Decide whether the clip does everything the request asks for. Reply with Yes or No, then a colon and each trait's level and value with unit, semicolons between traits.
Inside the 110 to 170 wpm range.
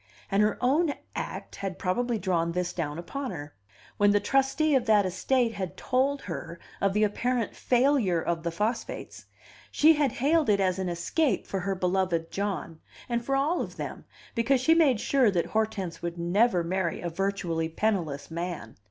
No: average, 180 wpm